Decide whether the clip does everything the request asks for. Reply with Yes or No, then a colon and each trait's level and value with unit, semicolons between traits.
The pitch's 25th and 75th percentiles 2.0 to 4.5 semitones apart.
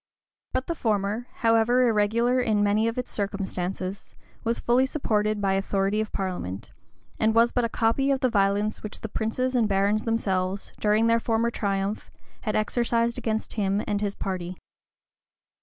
Yes: average, 2.7 semitones